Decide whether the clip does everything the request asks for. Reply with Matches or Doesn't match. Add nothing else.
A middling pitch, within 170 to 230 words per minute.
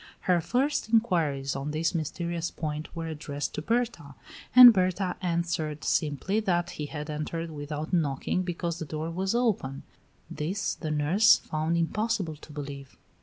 Doesn't match